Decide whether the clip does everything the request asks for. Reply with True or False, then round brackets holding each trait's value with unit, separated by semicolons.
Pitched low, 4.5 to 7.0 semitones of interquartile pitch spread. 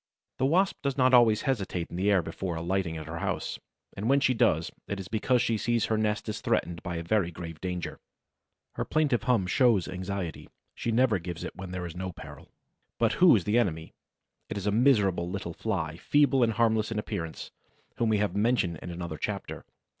True (100 Hz; 5.2 semitones)